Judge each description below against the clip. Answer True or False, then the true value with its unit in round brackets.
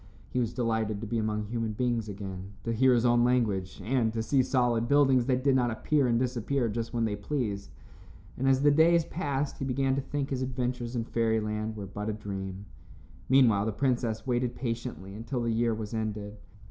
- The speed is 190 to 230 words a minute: True (200 wpm)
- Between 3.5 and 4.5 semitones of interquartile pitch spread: False (3.1 semitones)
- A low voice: True (120 Hz)